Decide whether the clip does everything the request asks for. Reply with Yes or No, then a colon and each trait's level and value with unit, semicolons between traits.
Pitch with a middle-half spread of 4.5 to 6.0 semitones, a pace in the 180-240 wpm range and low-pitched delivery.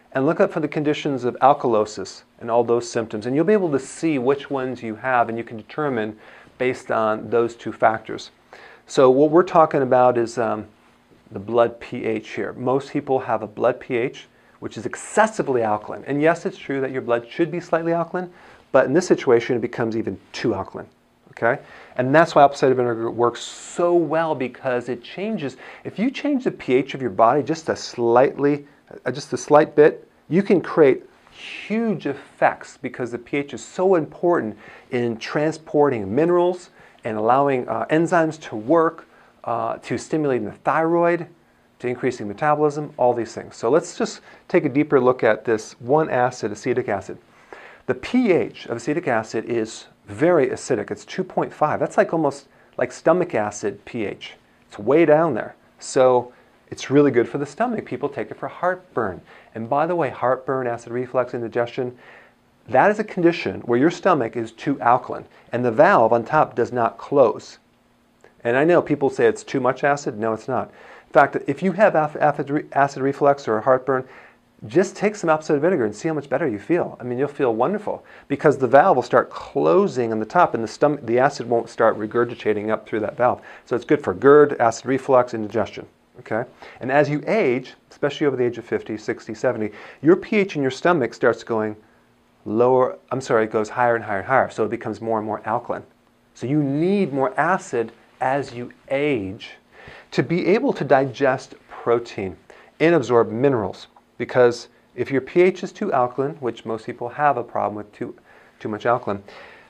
Yes: average, 5.1 semitones; average, 190 wpm; low, 130 Hz